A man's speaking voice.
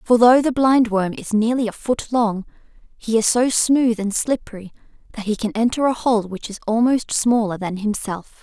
No: female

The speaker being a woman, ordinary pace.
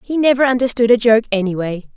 Yes: female; average, 185 wpm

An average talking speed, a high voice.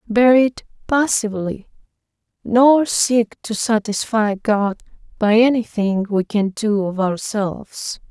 No: slow, 110 wpm; high, 220 Hz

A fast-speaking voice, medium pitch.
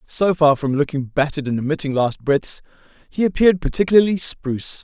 No: average, 160 wpm; medium, 155 Hz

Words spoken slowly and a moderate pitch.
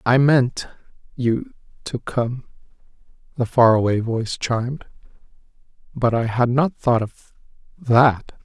No: slow, 90 wpm; low, 120 Hz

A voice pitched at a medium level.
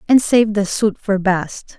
No: high, 205 Hz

